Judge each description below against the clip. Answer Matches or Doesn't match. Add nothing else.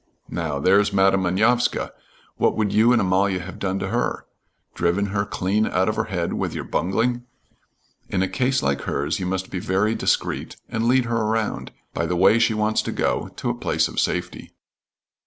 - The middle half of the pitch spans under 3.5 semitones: Matches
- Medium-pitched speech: Doesn't match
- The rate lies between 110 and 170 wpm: Doesn't match